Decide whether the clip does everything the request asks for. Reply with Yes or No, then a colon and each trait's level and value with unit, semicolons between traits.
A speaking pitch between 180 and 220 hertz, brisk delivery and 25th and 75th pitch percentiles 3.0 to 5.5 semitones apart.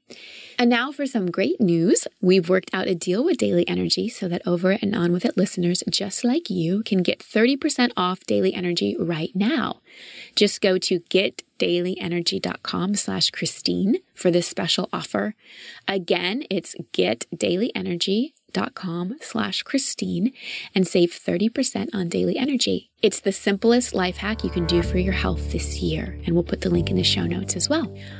No: medium, 185 Hz; average, 165 wpm; average, 3.4 semitones